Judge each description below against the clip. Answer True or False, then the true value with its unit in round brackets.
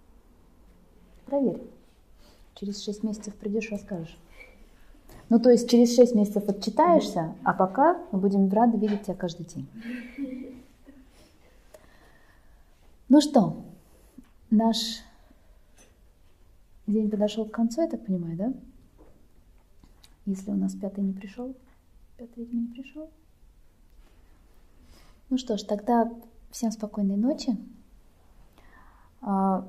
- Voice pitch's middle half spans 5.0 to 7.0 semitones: True (5.3 semitones)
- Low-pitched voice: False (210 Hz)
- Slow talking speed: True (100 wpm)